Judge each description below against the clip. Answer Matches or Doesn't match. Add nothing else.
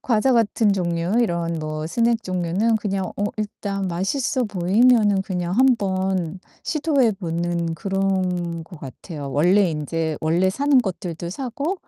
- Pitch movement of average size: Matches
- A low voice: Doesn't match